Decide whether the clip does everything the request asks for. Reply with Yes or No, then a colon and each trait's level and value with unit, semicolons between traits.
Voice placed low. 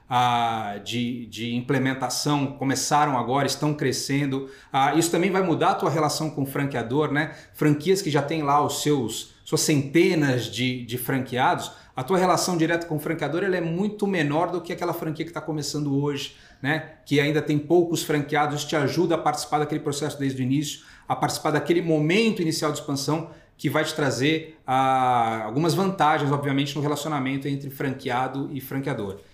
No: medium, 150 Hz